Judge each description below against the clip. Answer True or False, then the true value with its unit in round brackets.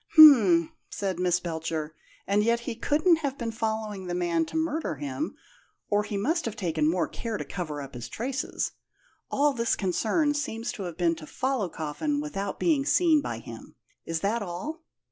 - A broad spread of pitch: True (8.2 semitones)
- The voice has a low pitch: False (210 Hz)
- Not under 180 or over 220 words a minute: True (185 wpm)